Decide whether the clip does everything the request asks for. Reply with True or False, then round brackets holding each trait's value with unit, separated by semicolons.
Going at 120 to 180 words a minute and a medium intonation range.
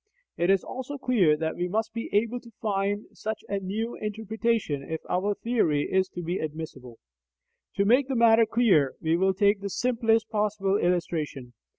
True (175 wpm; 4.5 semitones)